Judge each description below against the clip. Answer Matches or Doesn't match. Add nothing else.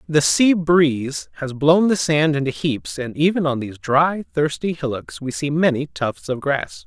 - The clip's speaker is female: Doesn't match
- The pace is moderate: Matches